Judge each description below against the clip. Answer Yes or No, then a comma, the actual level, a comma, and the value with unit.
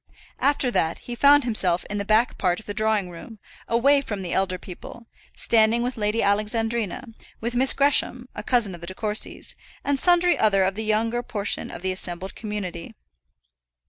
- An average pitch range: Yes, average, 3.8 semitones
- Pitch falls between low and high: No, high, 215 Hz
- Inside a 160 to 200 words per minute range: Yes, average, 180 wpm